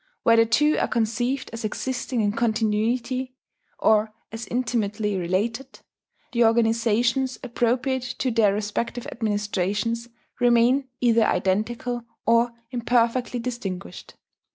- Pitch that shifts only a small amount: Yes, narrow, 2.2 semitones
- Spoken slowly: Yes, slow, 105 wpm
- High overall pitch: Yes, high, 230 Hz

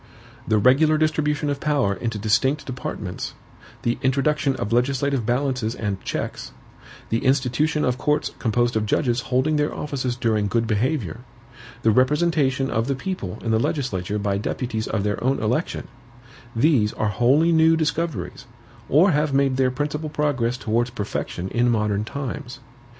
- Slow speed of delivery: No, average, 150 wpm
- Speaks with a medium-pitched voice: No, low, 130 Hz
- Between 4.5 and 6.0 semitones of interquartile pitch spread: Yes, average, 4.8 semitones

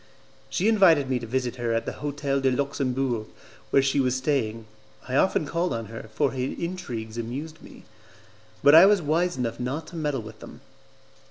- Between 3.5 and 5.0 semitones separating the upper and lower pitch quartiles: Yes, average, 4.5 semitones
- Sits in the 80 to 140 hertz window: Yes, low, 135 Hz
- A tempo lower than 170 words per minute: No, average, 185 wpm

